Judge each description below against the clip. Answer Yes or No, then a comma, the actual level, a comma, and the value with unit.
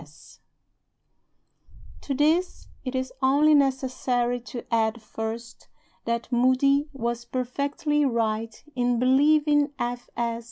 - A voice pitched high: Yes, very high, 255 Hz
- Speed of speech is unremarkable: No, slow, 115 wpm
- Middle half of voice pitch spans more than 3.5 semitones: No, average, 3.1 semitones